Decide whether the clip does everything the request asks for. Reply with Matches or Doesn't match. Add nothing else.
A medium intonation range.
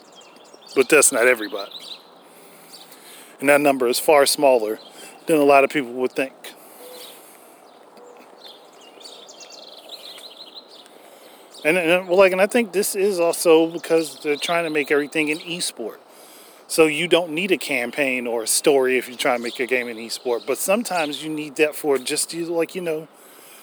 Matches